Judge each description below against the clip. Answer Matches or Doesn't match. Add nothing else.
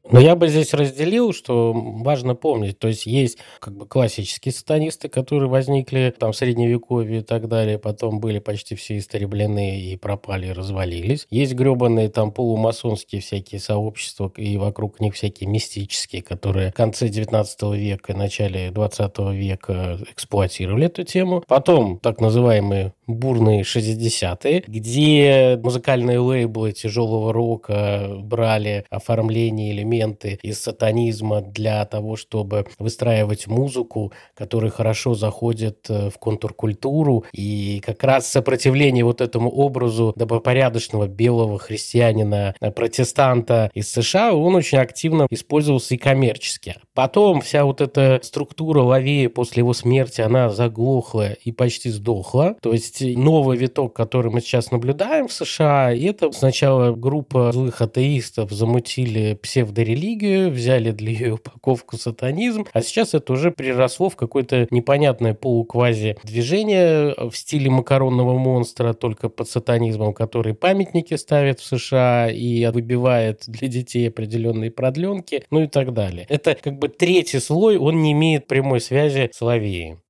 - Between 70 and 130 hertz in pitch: Matches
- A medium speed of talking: Matches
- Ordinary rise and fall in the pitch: Matches